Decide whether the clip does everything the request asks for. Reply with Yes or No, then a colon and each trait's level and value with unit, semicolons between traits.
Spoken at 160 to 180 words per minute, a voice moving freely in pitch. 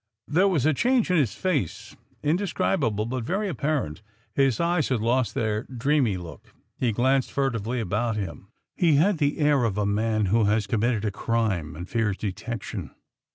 Yes: average, 170 wpm; wide, 5.8 semitones